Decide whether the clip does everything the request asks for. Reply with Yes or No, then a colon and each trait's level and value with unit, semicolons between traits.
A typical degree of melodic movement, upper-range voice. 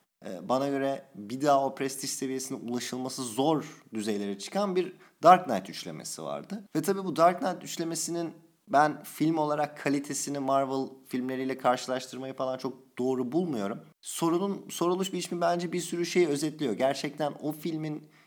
No: average, 4.3 semitones; medium, 145 Hz